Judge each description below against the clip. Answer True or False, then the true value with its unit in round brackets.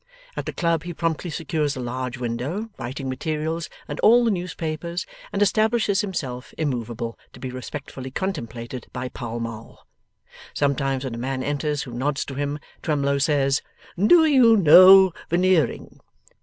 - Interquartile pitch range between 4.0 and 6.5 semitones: True (5.5 semitones)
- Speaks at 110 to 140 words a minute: False (150 wpm)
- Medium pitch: True (145 Hz)